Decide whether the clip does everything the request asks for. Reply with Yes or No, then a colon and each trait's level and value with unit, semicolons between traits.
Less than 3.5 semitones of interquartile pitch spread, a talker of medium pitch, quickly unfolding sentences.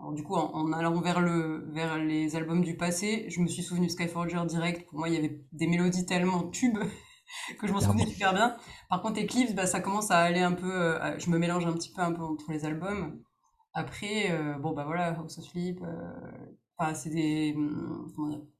Yes: narrow, 2.5 semitones; medium, 170 Hz; fast, 225 wpm